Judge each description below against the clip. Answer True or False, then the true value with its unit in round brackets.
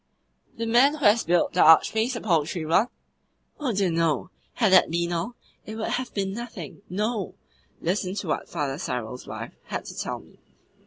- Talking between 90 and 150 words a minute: False (180 wpm)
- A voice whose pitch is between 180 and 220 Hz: True (190 Hz)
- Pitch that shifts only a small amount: False (5.2 semitones)